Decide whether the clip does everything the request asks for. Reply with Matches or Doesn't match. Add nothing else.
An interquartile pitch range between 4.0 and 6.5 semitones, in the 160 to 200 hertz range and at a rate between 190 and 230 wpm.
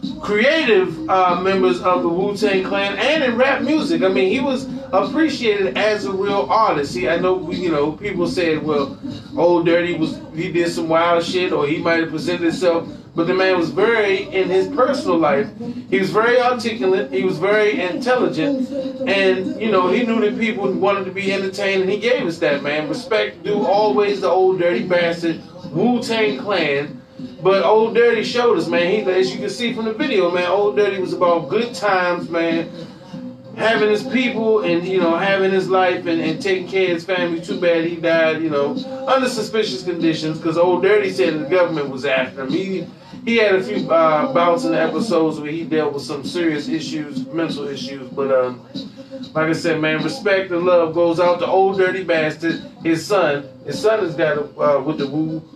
Matches